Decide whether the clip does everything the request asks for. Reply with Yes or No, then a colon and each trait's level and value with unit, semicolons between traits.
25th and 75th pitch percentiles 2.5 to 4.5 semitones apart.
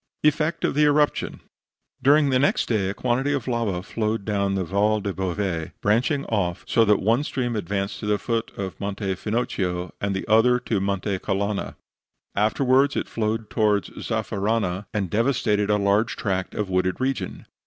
Yes: average, 3.5 semitones